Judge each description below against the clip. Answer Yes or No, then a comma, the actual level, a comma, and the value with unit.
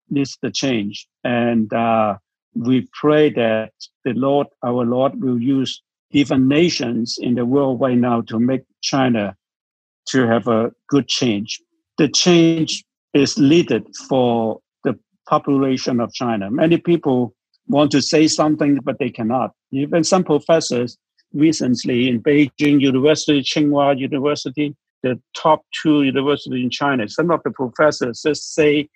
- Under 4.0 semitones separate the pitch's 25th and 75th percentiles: Yes, average, 3.5 semitones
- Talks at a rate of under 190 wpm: Yes, average, 140 wpm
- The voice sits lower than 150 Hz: Yes, low, 135 Hz